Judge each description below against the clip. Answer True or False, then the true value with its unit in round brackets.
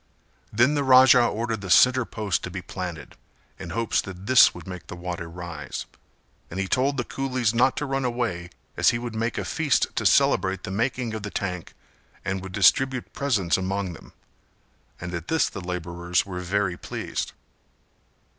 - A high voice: False (100 Hz)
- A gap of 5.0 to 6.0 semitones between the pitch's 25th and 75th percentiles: True (5.6 semitones)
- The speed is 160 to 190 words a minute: True (180 wpm)